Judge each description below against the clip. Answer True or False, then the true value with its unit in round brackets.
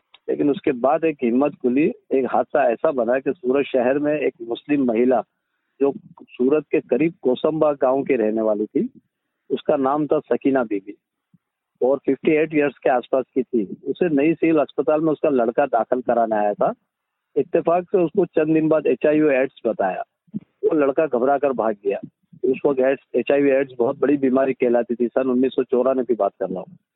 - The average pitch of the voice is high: False (135 Hz)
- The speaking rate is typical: True (180 wpm)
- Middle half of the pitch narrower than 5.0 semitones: True (3.4 semitones)